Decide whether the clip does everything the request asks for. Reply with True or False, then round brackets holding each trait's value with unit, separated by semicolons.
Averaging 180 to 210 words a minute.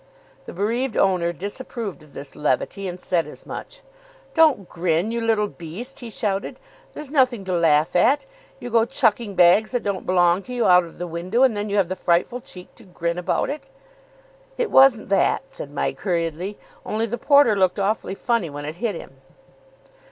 True (190 wpm)